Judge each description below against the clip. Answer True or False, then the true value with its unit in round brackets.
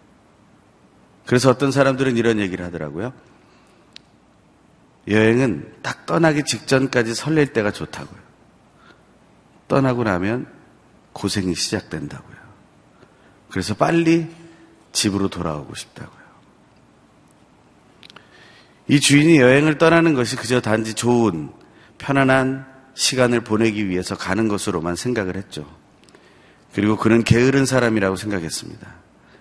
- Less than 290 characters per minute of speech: True (260 characters per minute)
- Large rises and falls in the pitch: False (4.9 semitones)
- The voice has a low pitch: True (115 Hz)